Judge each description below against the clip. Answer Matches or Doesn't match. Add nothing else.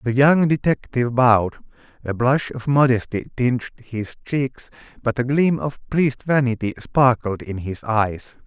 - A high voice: Doesn't match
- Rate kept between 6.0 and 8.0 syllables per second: Doesn't match